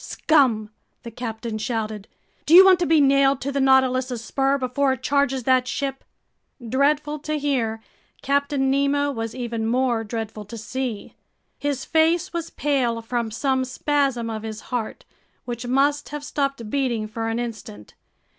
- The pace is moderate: Yes, average, 155 wpm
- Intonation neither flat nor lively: Yes, average, 3.7 semitones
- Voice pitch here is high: Yes, very high, 260 Hz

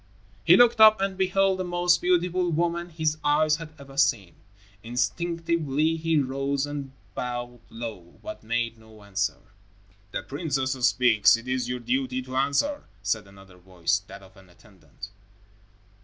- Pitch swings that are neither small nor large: No, wide, 6.8 semitones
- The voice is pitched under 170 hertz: Yes, low, 135 Hz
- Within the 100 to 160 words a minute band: Yes, average, 150 wpm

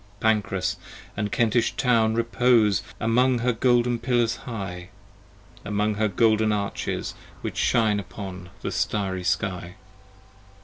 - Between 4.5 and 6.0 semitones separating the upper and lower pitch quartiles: No, average, 3.1 semitones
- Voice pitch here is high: No, low, 110 Hz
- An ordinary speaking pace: No, slow, 115 wpm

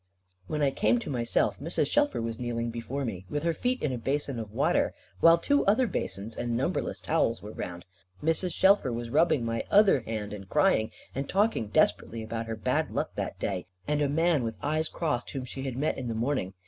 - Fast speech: Yes, fast, 210 wpm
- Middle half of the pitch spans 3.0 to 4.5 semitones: No, wide, 5.4 semitones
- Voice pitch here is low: Yes, low, 125 Hz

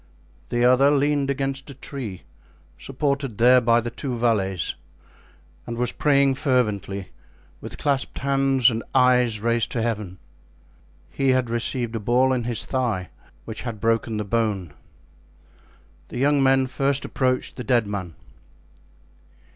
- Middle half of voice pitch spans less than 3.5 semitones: Yes, average, 3.1 semitones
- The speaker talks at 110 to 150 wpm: Yes, average, 140 wpm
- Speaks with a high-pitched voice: No, low, 125 Hz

